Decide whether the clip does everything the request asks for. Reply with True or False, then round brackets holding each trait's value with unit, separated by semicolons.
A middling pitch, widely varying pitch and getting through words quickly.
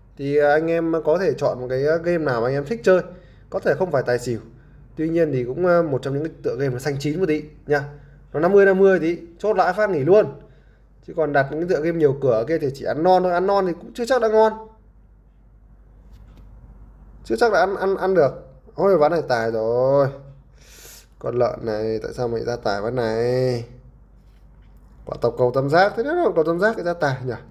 True (150 Hz; 5.9 semitones; 230 wpm)